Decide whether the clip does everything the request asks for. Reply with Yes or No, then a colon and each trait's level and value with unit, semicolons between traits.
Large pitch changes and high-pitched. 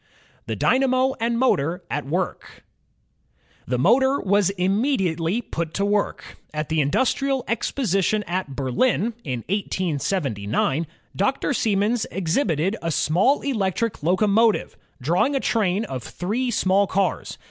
Yes: wide, 6.0 semitones; high, 195 Hz